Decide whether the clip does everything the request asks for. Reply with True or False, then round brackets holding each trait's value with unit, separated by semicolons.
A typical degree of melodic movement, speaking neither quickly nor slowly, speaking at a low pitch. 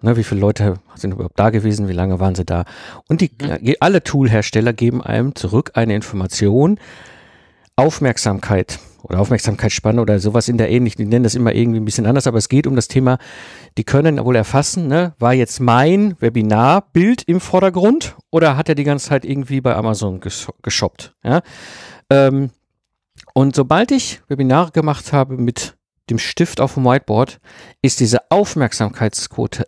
True (4.5 semitones; 170 wpm; 120 Hz)